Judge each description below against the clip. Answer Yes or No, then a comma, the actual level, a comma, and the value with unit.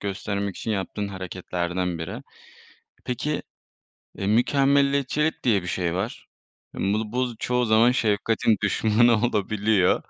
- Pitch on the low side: Yes, low, 105 Hz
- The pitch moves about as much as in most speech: Yes, average, 4.0 semitones